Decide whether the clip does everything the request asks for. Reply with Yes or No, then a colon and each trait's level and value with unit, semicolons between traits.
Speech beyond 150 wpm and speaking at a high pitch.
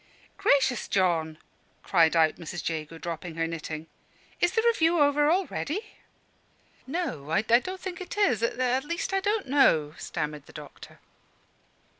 No: average, 140 wpm; high, 235 Hz